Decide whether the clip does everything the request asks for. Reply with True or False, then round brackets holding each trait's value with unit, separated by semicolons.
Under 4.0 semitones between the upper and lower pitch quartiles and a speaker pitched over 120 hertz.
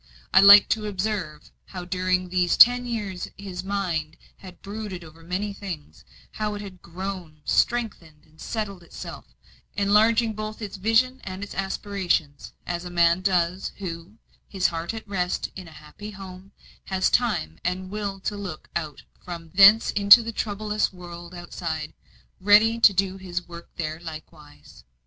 True (3.1 semitones; 185 Hz)